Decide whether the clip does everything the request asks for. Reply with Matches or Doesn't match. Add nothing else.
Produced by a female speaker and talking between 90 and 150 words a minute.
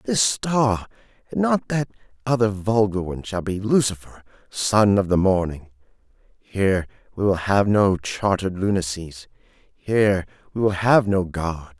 Doesn't match